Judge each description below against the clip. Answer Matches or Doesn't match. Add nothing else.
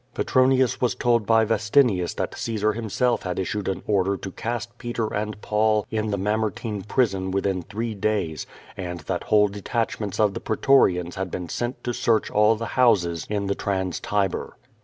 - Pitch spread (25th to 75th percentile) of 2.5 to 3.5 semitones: Matches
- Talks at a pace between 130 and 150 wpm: Doesn't match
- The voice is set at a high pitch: Doesn't match